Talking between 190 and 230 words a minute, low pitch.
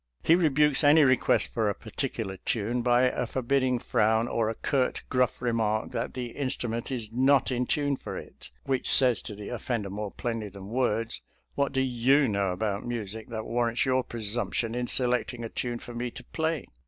Yes: fast, 205 wpm; low, 120 Hz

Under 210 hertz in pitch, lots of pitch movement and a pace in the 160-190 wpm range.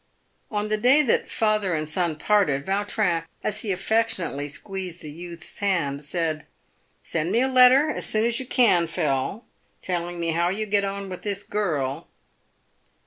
No: high, 190 Hz; average, 4.4 semitones; average, 170 wpm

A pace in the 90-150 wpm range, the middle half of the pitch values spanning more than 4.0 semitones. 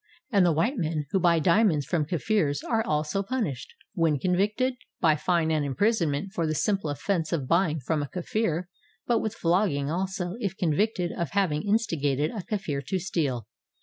No: average, 180 wpm; average, 4.8 semitones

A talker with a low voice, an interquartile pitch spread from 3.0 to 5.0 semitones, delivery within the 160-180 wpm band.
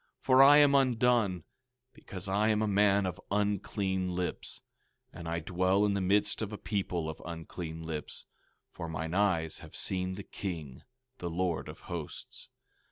Yes: very low, 95 Hz; average, 3.4 semitones; average, 165 wpm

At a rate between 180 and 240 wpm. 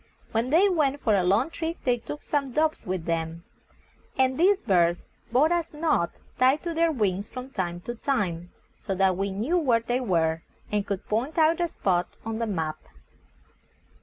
Yes: average, 185 wpm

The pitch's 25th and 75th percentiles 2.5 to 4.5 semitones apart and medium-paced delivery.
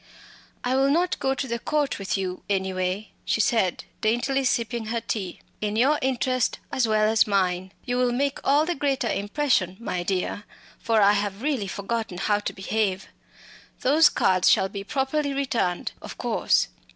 No: average, 5.3 semitones; average, 170 wpm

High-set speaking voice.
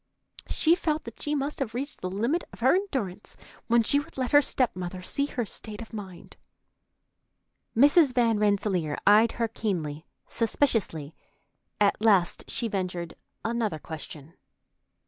Yes: high, 220 Hz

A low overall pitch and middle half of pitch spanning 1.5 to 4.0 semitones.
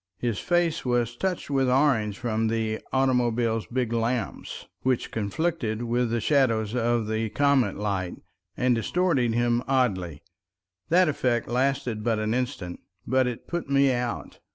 Yes: low, 120 Hz; average, 3.0 semitones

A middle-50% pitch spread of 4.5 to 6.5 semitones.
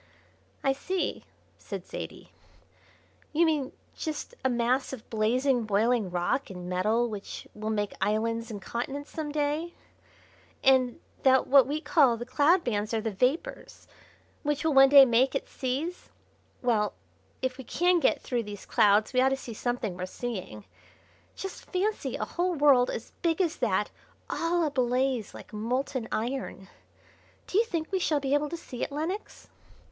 Yes: average, 4.9 semitones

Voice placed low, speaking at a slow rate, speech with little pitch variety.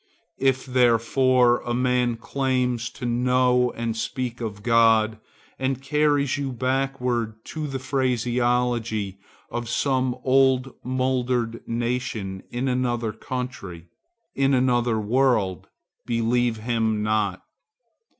Yes: low, 125 Hz; slow, 105 wpm; narrow, 2.1 semitones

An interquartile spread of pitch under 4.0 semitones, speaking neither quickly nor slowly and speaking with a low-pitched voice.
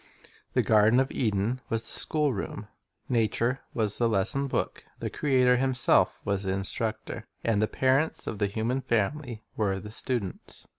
Yes: average, 3.6 semitones; average, 155 wpm; low, 115 Hz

